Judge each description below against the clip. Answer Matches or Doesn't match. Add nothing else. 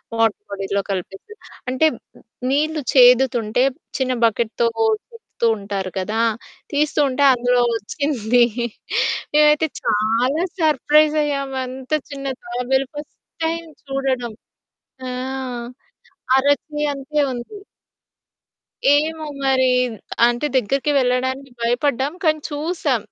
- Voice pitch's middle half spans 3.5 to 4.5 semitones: Matches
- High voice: Matches